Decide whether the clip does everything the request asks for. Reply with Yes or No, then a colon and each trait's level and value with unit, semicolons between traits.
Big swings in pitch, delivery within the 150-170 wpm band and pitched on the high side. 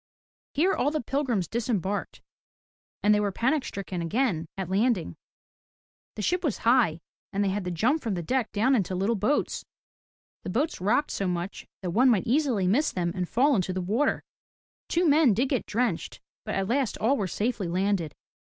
No: wide, 5.8 semitones; average, 185 wpm; high, 215 Hz